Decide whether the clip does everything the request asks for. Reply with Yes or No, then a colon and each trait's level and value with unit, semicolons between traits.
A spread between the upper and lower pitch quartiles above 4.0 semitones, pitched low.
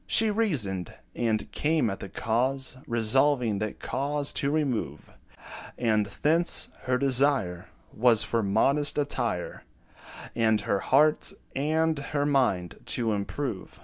Yes: average, 5.2 semitones; low, 125 Hz